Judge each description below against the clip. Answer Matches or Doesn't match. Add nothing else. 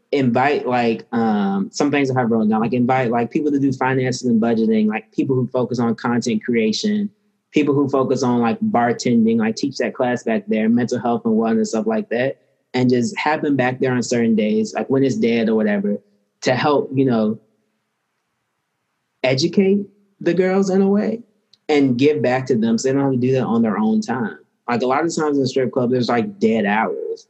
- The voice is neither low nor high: Doesn't match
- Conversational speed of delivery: Doesn't match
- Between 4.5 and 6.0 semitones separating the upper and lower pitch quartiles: Matches